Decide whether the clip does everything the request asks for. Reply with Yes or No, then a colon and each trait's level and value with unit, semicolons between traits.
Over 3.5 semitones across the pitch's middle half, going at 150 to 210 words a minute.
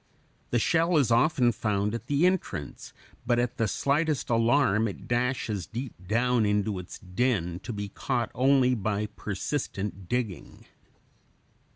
No: average, 4.0 semitones; average, 140 wpm